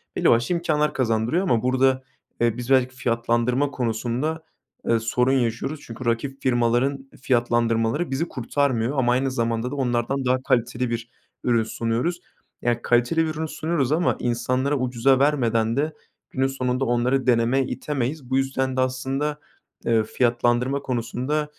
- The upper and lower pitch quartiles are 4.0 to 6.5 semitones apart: No, narrow, 2.6 semitones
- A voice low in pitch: Yes, low, 125 Hz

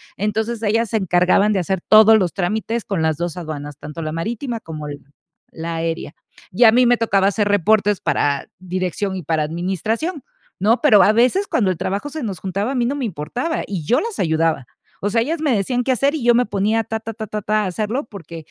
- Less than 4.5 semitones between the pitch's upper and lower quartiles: No, average, 4.9 semitones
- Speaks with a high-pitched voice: Yes, high, 205 Hz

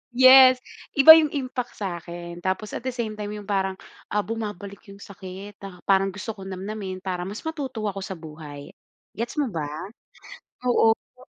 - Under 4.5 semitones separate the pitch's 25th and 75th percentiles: Yes, average, 3.7 semitones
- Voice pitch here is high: Yes, high, 200 Hz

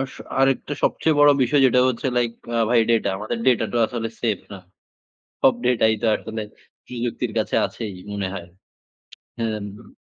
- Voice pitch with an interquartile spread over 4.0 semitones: No, narrow, 2.4 semitones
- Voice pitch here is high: No, low, 115 Hz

